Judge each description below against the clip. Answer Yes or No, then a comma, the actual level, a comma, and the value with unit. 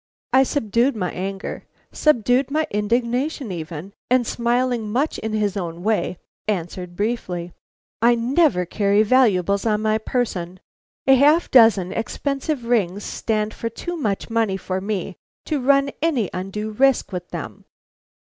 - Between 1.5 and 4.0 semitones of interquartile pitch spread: No, average, 4.7 semitones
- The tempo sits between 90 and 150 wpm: Yes, average, 140 wpm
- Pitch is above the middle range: Yes, high, 220 Hz